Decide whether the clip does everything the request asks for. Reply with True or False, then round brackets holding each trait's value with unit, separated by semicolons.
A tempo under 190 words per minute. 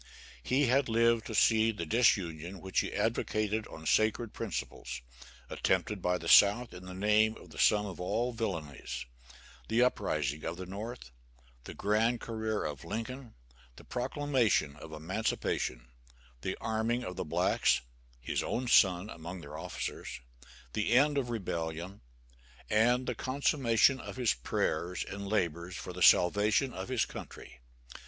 True (150 wpm)